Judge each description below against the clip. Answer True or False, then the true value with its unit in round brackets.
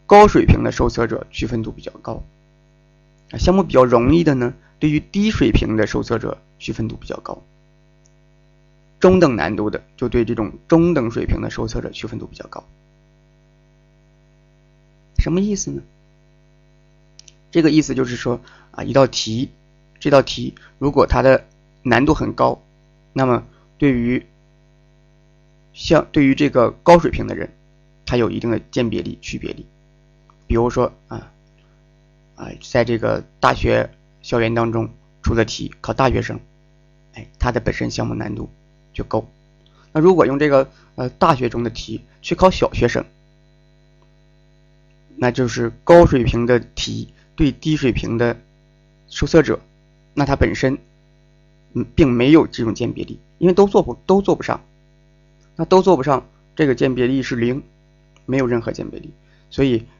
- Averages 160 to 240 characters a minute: True (220 characters per minute)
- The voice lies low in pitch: False (155 Hz)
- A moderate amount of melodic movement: True (4.1 semitones)